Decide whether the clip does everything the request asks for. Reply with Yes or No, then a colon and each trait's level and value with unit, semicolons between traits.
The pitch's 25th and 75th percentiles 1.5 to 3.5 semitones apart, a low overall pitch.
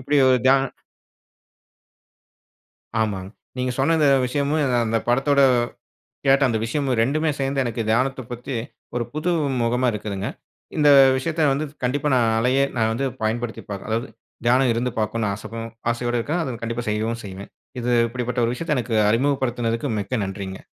Yes: average, 3.2 semitones; low, 125 Hz